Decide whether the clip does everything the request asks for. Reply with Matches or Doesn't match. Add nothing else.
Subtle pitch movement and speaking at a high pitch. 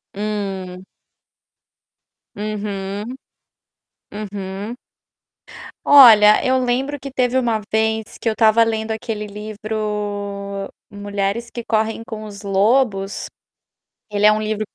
Matches